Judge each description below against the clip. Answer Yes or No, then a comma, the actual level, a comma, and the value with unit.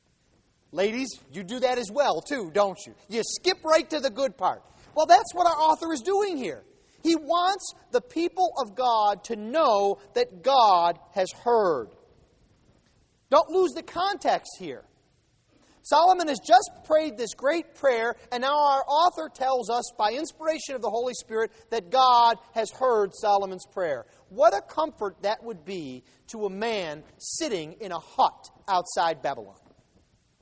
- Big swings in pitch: Yes, wide, 6.9 semitones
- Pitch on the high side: Yes, very high, 265 Hz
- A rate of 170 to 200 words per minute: No, average, 160 wpm